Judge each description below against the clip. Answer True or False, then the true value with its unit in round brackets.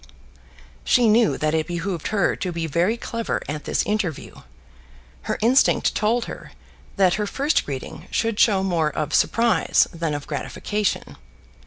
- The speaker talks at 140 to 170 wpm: True (150 wpm)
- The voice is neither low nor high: False (195 Hz)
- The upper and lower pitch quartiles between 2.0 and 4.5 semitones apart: False (5.5 semitones)